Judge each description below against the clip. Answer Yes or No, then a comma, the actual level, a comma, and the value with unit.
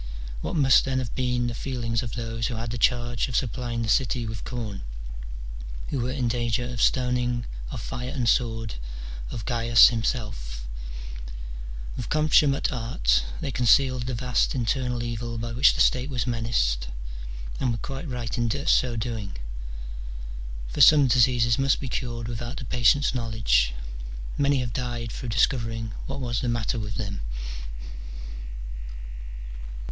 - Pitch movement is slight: Yes, narrow, 1.9 semitones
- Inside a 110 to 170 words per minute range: Yes, average, 150 wpm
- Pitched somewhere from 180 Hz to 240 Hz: No, low, 120 Hz